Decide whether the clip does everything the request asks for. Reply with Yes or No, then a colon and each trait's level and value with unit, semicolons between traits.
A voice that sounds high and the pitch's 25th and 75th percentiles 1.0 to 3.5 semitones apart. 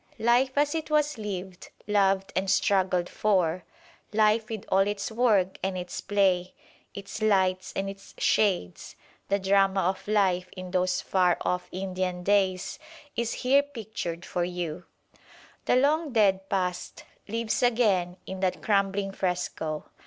Yes: high, 195 Hz; average, 2.8 semitones